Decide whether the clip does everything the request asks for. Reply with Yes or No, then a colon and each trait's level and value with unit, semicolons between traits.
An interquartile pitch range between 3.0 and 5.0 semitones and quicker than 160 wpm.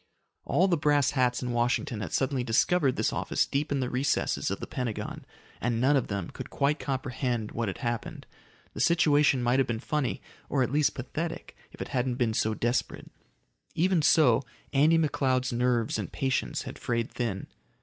Yes: average, 3.4 semitones; average, 180 wpm